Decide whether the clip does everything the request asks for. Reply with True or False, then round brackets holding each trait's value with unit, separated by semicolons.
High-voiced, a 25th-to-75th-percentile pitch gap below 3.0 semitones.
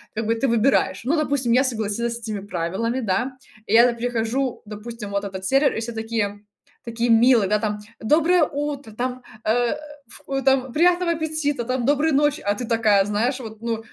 False (235 Hz; 3.7 semitones)